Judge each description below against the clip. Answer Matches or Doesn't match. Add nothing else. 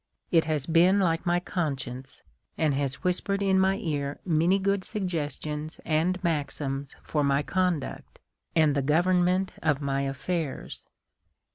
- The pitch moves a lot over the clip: Doesn't match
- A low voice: Doesn't match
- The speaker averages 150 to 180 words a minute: Doesn't match